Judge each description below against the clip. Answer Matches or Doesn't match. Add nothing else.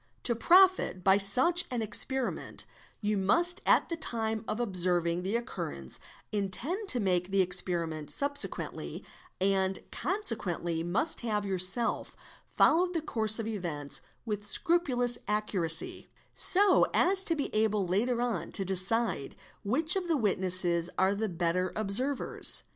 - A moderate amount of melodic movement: Doesn't match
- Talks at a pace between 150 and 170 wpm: Doesn't match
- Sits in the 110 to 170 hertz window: Doesn't match